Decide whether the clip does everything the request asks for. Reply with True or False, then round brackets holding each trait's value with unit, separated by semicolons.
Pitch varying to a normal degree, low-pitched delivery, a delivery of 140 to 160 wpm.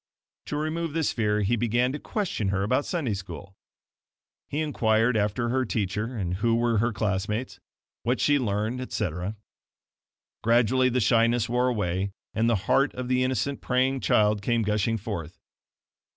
True (3.7 semitones; 115 Hz; 155 wpm)